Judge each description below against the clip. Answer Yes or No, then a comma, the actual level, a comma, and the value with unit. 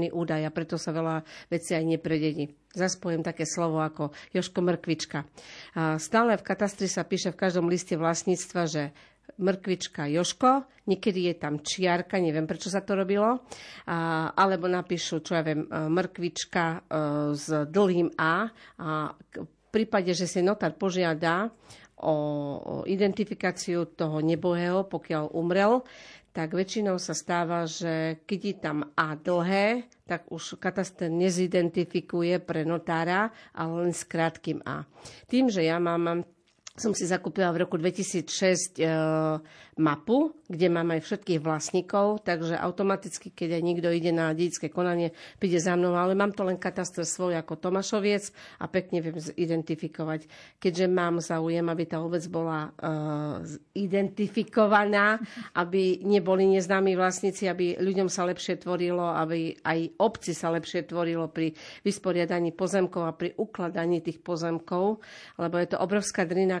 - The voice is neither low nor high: Yes, medium, 175 Hz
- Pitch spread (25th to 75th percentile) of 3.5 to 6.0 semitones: No, narrow, 2.6 semitones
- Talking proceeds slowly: No, average, 140 wpm